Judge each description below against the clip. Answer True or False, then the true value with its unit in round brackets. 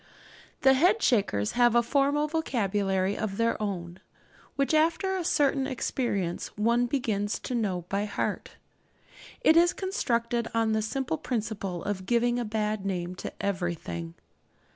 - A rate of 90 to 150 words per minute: True (140 wpm)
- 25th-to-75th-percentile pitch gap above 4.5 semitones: True (5.3 semitones)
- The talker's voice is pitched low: False (225 Hz)